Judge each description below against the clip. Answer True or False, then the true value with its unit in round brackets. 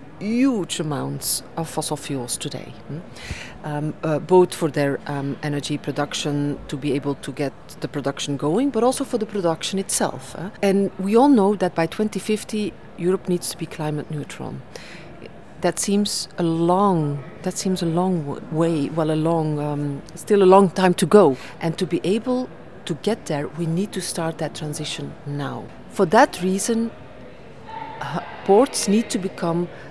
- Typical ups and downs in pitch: True (4.8 semitones)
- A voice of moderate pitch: True (170 Hz)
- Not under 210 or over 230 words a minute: False (175 wpm)